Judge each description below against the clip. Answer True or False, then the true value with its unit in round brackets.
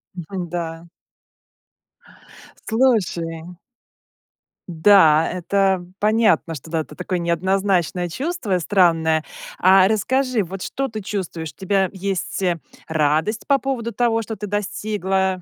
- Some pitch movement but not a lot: True (3.8 semitones)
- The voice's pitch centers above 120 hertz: True (190 Hz)